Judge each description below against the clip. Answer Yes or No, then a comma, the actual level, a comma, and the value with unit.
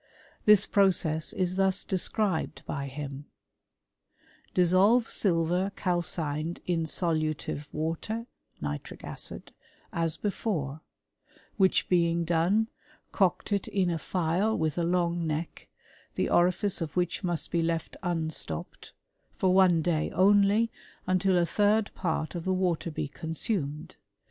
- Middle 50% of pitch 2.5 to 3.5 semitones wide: Yes, average, 3.0 semitones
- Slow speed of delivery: Yes, slow, 130 wpm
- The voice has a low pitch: No, medium, 175 Hz